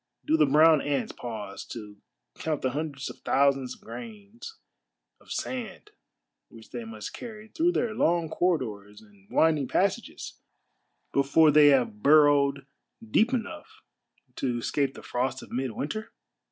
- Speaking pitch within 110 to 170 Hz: Yes, medium, 140 Hz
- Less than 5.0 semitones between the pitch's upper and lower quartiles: No, wide, 5.6 semitones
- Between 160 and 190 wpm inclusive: No, average, 140 wpm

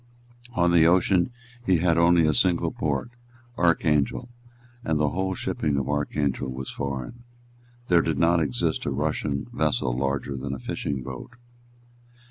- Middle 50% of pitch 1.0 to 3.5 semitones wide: No, average, 4.0 semitones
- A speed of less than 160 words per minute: Yes, average, 145 wpm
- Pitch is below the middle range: Yes, very low, 75 Hz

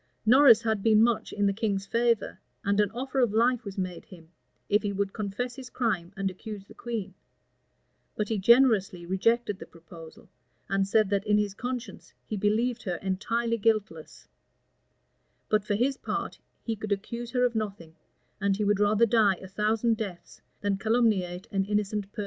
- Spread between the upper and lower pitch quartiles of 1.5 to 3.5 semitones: Yes, average, 2.9 semitones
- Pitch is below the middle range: No, high, 210 Hz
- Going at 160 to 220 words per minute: Yes, average, 180 wpm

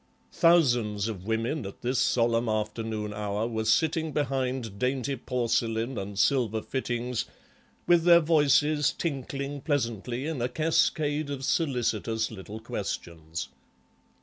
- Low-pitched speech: Yes, low, 120 Hz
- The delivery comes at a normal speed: No, slow, 120 wpm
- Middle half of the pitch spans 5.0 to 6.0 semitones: No, average, 4.5 semitones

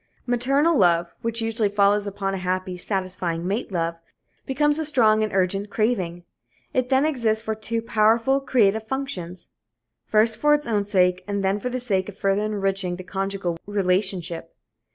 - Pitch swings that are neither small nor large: Yes, average, 3.8 semitones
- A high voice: Yes, high, 205 Hz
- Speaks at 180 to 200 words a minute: No, average, 165 wpm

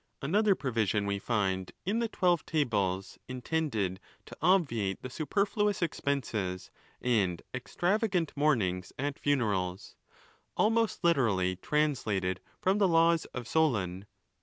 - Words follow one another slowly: Yes, slow, 110 wpm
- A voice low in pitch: Yes, low, 130 Hz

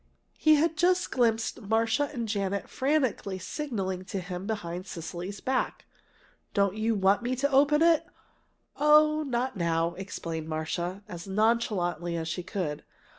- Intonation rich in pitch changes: Yes, wide, 6.7 semitones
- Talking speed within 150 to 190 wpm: No, average, 140 wpm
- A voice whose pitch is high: Yes, high, 205 Hz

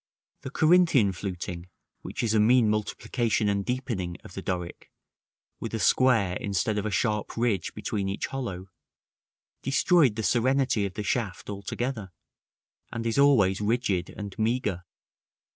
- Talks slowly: No, average, 145 wpm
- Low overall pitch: Yes, low, 105 Hz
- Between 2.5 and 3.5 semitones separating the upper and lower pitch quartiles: No, average, 4.3 semitones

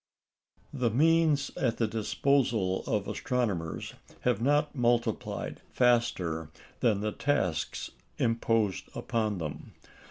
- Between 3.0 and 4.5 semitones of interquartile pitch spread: Yes, average, 4.2 semitones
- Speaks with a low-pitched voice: Yes, low, 115 Hz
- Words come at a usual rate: No, slow, 100 wpm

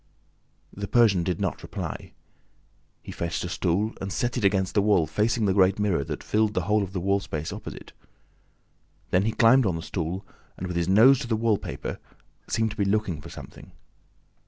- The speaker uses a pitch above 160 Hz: No, low, 100 Hz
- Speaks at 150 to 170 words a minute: No, average, 195 wpm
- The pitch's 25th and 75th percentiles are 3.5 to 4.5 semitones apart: No, average, 3.1 semitones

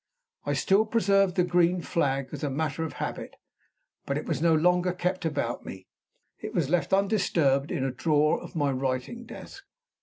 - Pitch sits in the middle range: Yes, medium, 160 Hz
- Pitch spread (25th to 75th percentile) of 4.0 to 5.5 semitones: Yes, average, 4.6 semitones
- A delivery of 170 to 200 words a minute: Yes, average, 180 wpm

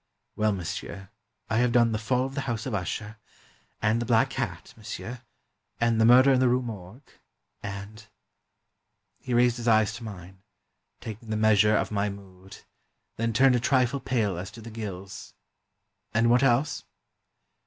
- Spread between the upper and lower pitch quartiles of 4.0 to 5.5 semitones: No, average, 3.0 semitones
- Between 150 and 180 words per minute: Yes, average, 175 wpm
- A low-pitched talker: Yes, low, 115 Hz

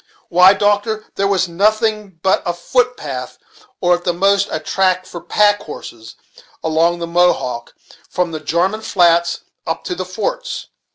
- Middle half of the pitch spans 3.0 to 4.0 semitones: Yes, average, 3.3 semitones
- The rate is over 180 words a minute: No, average, 160 wpm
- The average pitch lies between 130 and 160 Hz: No, medium, 180 Hz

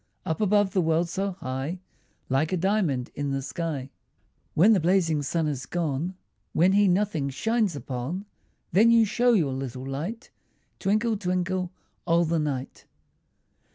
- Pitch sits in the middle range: Yes, medium, 170 Hz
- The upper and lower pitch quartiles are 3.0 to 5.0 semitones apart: No, wide, 5.6 semitones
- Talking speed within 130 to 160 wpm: Yes, average, 150 wpm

